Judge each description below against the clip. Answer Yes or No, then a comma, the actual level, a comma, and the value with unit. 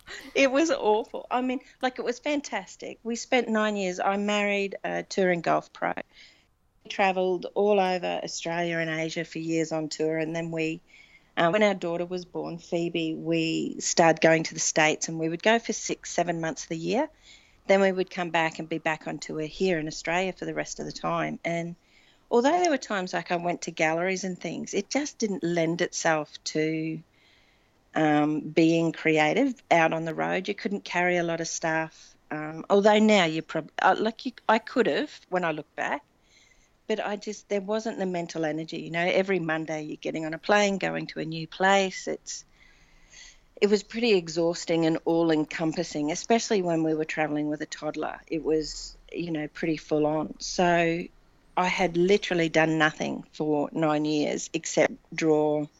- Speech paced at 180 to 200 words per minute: Yes, average, 190 wpm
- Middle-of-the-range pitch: Yes, medium, 170 Hz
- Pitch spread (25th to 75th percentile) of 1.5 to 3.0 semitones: No, average, 3.8 semitones